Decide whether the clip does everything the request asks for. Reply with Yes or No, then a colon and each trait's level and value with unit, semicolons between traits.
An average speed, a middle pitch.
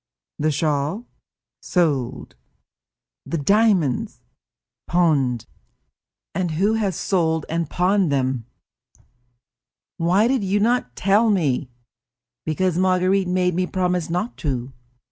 No: slow, 105 wpm; medium, 180 Hz